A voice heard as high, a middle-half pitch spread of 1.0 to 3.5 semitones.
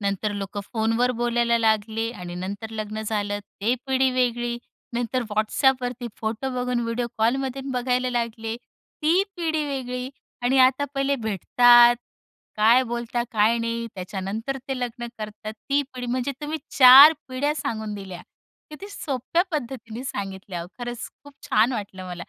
Yes: high, 240 Hz; average, 3.0 semitones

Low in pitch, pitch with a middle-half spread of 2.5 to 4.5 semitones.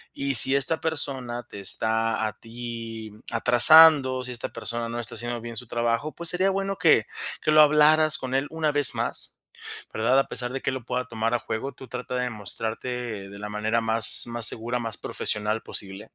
Yes: low, 120 Hz; average, 3.4 semitones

